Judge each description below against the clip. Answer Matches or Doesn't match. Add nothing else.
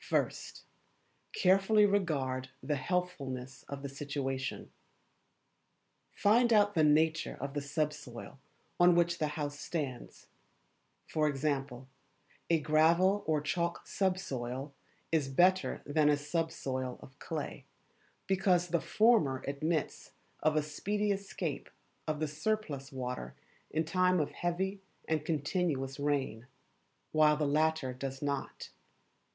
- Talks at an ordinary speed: Doesn't match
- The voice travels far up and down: Doesn't match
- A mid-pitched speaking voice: Matches